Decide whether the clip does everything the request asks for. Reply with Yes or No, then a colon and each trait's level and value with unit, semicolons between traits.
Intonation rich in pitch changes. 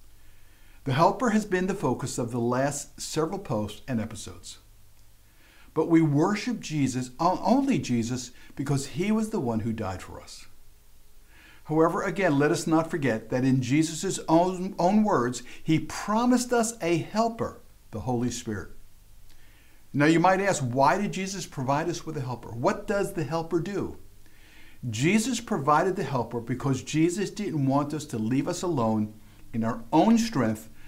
Yes: wide, 8.0 semitones